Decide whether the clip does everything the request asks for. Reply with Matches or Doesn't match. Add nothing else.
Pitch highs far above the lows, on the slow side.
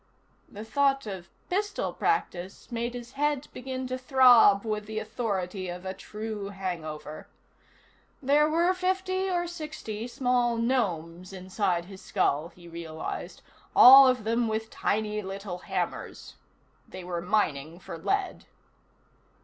Matches